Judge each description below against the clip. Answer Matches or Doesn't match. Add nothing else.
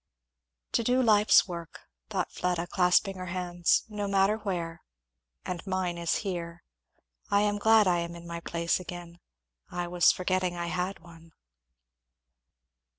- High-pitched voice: Doesn't match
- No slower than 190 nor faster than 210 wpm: Doesn't match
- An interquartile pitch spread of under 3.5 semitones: Matches